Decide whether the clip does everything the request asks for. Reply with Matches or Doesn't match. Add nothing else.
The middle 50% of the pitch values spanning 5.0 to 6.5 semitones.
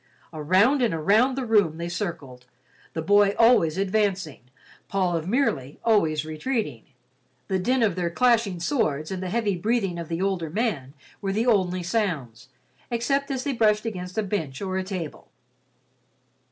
Matches